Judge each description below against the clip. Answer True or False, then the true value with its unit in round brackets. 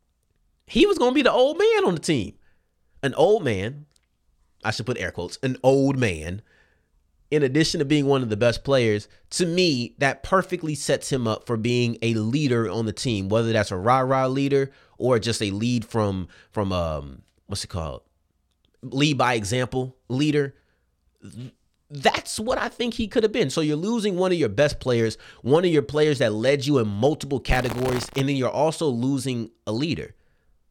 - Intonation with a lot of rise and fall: True (5.9 semitones)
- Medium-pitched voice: False (125 Hz)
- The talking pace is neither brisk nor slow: True (190 wpm)